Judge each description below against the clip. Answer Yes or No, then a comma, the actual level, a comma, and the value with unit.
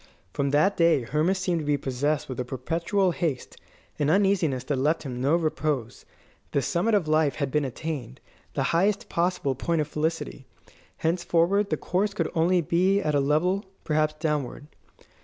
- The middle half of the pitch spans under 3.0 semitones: No, average, 3.8 semitones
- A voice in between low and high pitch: Yes, medium, 155 Hz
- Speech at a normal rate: Yes, average, 170 wpm